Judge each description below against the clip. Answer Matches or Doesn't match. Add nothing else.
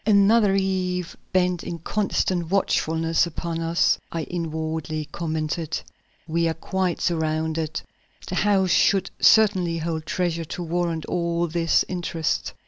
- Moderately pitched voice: Matches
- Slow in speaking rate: Matches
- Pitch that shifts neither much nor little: Doesn't match